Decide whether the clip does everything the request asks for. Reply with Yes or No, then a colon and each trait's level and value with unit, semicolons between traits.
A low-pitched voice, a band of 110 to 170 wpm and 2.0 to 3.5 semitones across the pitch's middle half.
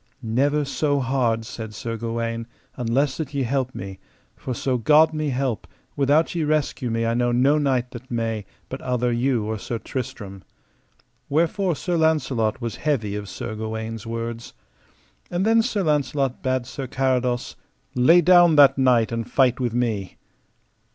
No: low, 125 Hz; average, 160 wpm; average, 3.9 semitones